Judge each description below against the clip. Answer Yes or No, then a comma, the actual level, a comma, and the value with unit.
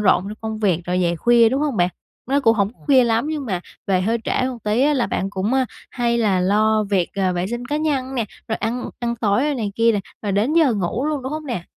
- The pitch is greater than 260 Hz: No, high, 230 Hz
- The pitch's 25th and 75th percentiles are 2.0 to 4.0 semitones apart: No, average, 4.6 semitones